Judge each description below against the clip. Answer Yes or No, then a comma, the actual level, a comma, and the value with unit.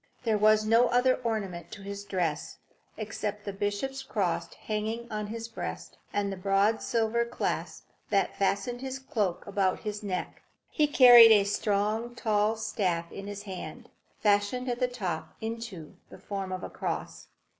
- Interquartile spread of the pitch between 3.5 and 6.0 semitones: No, average, 2.7 semitones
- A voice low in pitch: No, high, 210 Hz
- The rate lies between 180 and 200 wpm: No, average, 160 wpm